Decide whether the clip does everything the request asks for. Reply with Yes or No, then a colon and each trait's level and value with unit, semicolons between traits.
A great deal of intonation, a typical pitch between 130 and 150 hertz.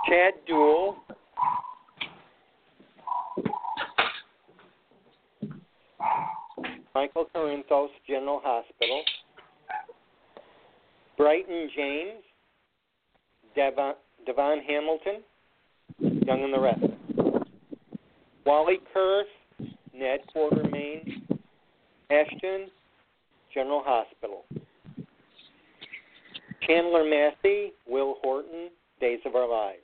No: wide, 6.4 semitones; medium, 160 Hz